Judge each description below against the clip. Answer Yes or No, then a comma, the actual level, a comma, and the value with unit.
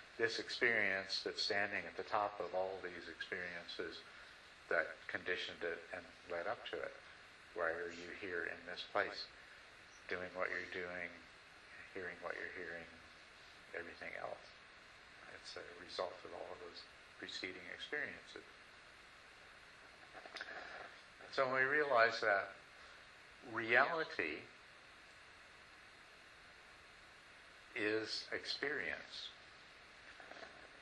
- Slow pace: Yes, slow, 105 wpm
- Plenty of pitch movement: No, average, 3.5 semitones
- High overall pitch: No, very low, 90 Hz